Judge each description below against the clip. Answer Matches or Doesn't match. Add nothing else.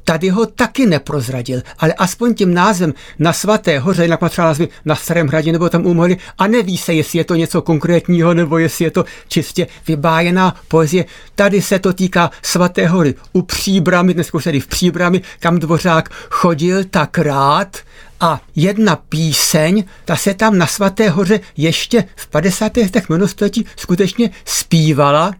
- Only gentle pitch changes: Doesn't match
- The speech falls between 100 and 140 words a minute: Doesn't match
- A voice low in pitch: Doesn't match